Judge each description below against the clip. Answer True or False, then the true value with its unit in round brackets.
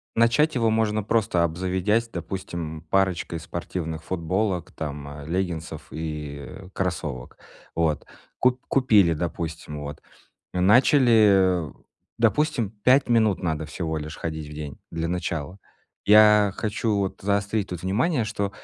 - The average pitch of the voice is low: True (95 Hz)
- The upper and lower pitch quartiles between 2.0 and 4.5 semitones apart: False (5.0 semitones)